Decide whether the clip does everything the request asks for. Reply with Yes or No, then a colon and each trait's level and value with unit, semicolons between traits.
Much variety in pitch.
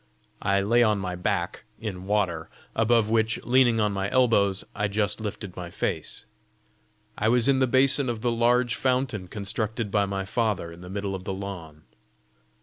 No: average, 3.4 semitones